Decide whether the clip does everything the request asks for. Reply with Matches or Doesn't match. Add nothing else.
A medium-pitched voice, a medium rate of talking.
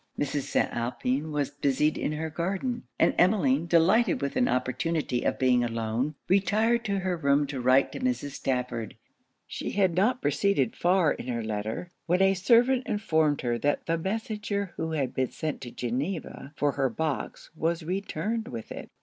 Matches